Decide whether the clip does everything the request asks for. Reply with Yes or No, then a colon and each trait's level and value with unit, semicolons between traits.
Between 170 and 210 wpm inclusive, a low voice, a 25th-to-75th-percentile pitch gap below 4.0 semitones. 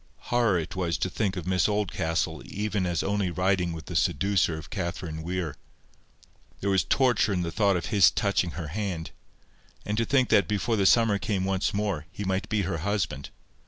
Yes: average, 195 wpm; very low, 95 Hz; average, 3.1 semitones